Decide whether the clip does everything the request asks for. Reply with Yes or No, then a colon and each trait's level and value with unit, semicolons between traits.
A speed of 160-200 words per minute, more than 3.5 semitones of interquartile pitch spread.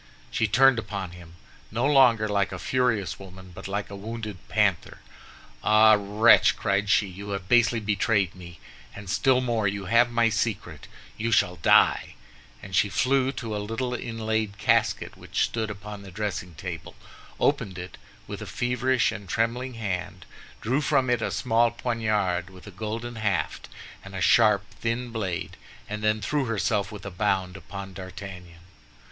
No: average, 165 wpm; average, 3.2 semitones